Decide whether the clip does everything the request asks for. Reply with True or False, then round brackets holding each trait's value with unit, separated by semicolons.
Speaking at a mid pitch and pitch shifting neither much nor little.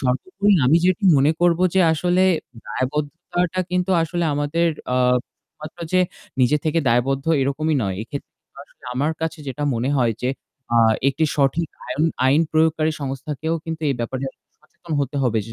True (150 Hz; 3.9 semitones)